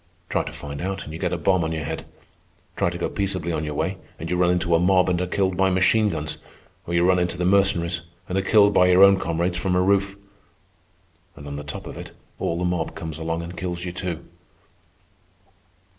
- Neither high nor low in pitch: No, very low, 90 Hz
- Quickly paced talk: Yes, fast, 235 wpm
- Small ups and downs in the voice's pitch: Yes, narrow, 2.1 semitones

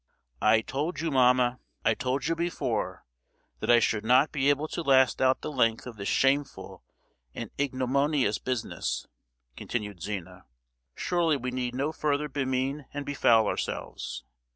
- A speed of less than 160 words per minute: Yes, average, 145 wpm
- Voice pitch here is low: Yes, low, 130 Hz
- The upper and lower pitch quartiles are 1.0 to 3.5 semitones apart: Yes, average, 3.0 semitones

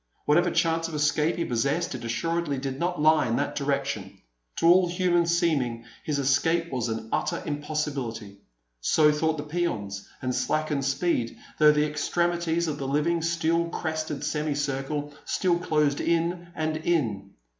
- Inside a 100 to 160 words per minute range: Yes, average, 155 wpm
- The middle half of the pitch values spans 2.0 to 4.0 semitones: Yes, average, 3.6 semitones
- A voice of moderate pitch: Yes, medium, 150 Hz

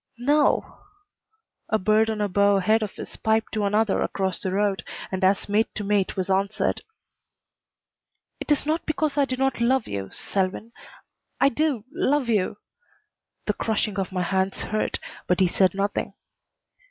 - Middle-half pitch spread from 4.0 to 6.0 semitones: No, average, 3.2 semitones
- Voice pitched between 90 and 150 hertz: No, high, 210 Hz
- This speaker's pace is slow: No, average, 165 wpm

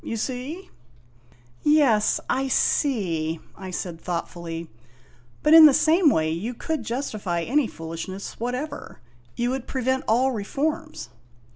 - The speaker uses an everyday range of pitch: No, wide, 8.5 semitones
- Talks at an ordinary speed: No, slow, 130 wpm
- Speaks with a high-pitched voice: Yes, high, 235 Hz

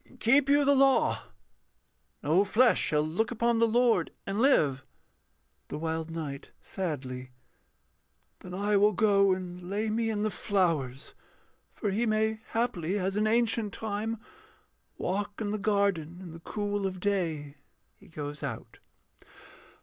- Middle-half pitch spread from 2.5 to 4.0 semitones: No, average, 4.9 semitones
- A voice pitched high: Yes, high, 200 Hz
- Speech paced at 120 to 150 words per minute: Yes, average, 140 wpm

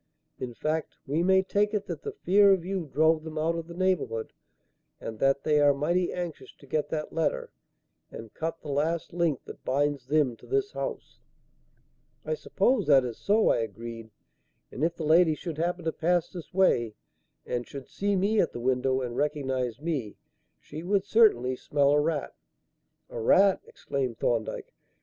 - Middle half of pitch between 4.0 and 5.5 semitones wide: Yes, average, 5.2 semitones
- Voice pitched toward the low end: No, medium, 155 Hz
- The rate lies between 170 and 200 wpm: Yes, average, 180 wpm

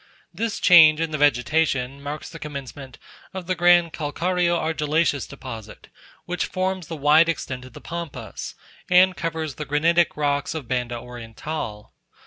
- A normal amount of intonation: Yes, average, 3.9 semitones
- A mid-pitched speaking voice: Yes, medium, 155 Hz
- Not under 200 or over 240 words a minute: No, average, 145 wpm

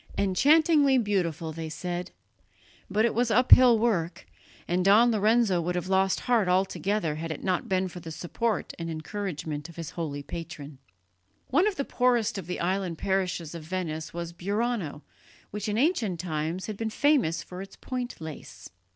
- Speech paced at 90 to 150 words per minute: No, average, 170 wpm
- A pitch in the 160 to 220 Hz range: Yes, medium, 185 Hz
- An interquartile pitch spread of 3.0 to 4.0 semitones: No, average, 5.0 semitones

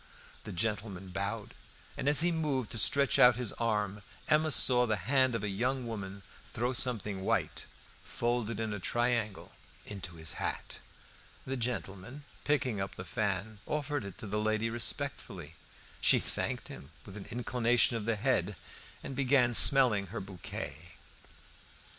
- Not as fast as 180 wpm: Yes, average, 155 wpm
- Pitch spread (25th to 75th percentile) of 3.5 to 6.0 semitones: Yes, average, 4.1 semitones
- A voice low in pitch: Yes, low, 115 Hz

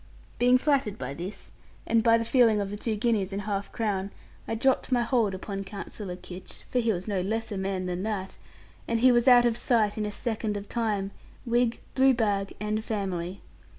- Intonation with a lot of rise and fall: No, average, 3.0 semitones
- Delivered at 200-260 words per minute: Yes, fast, 205 wpm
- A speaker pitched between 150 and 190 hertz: No, high, 215 Hz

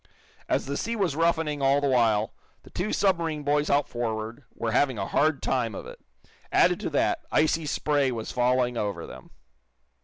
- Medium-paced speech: Yes, average, 180 wpm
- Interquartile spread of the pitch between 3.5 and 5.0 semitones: Yes, average, 4.5 semitones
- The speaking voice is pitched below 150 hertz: Yes, low, 135 Hz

